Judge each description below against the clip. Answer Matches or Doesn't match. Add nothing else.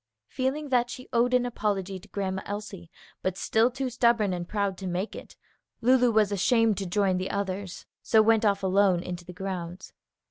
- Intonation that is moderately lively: Matches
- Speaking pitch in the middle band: Doesn't match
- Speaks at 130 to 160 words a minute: Doesn't match